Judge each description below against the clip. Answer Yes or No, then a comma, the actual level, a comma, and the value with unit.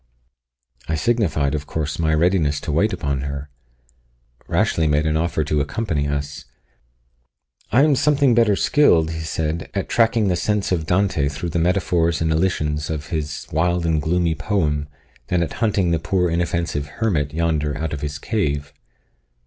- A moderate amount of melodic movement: Yes, average, 3.5 semitones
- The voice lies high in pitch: No, very low, 80 Hz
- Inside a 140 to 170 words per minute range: Yes, average, 165 wpm